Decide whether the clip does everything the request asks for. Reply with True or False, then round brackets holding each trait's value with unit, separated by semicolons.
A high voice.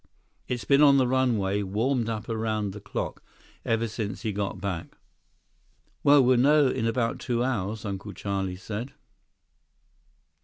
False (115 Hz)